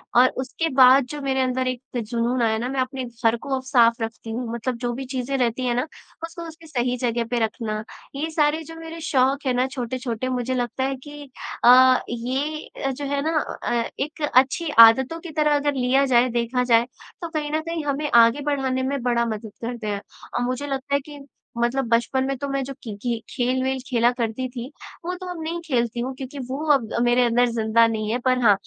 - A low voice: No, very high, 255 Hz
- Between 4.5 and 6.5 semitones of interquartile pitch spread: No, average, 2.8 semitones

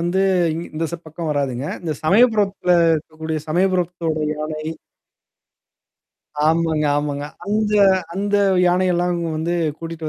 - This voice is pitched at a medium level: Yes, medium, 165 Hz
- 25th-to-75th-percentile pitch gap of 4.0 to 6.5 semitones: No, average, 2.8 semitones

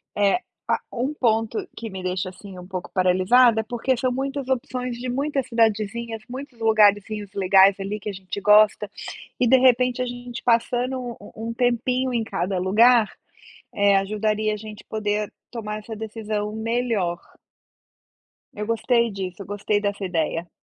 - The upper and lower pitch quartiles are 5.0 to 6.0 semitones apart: No, average, 3.3 semitones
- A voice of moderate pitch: No, high, 220 Hz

